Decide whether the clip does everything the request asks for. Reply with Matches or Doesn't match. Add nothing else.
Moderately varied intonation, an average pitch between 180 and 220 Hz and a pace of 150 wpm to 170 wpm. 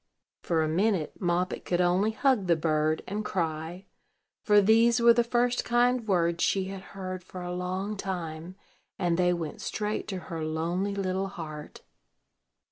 Matches